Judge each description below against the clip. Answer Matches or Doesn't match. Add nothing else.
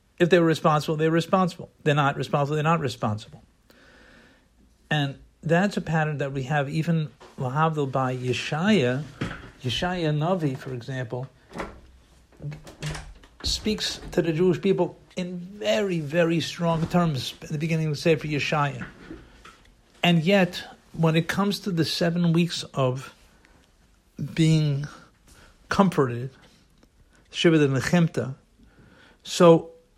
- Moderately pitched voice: Matches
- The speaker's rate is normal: Doesn't match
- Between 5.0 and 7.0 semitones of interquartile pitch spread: Doesn't match